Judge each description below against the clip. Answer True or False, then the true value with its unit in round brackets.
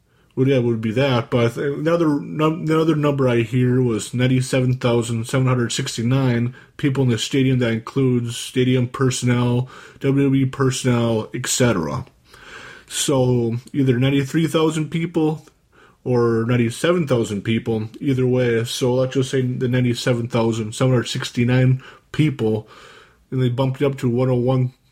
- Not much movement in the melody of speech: True (2.3 semitones)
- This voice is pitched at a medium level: False (130 Hz)